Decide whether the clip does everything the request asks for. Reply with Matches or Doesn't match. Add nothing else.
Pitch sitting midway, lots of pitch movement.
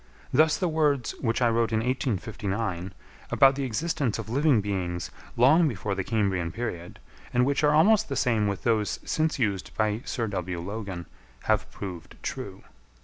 Doesn't match